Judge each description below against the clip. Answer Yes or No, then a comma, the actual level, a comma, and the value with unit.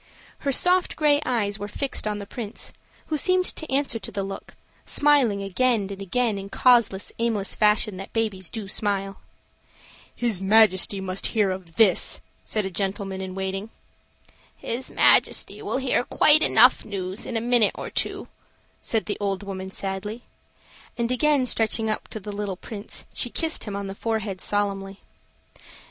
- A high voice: Yes, high, 210 Hz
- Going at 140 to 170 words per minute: Yes, average, 165 wpm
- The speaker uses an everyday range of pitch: Yes, average, 3.5 semitones